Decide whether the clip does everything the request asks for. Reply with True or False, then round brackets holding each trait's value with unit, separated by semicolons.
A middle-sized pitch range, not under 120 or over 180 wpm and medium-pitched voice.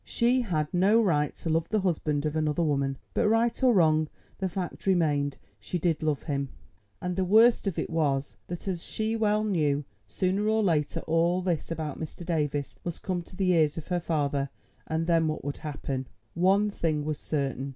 False (4.1 semitones; 195 wpm; 165 Hz)